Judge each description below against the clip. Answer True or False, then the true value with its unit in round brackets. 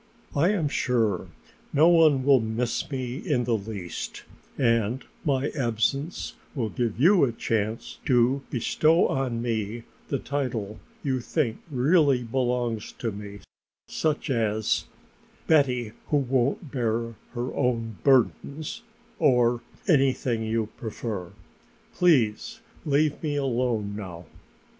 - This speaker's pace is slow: True (120 wpm)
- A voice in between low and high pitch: False (125 Hz)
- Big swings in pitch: False (3.9 semitones)